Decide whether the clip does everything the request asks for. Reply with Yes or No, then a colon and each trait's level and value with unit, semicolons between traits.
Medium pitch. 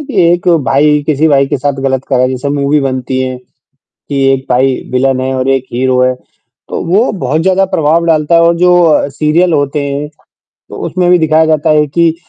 Yes: medium, 145 Hz